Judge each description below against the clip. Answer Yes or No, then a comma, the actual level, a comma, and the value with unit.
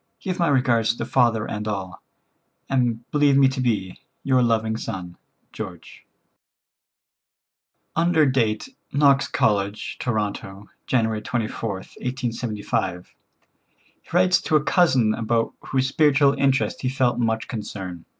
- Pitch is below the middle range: Yes, low, 120 Hz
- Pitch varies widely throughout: No, average, 4.2 semitones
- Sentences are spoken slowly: Yes, slow, 120 wpm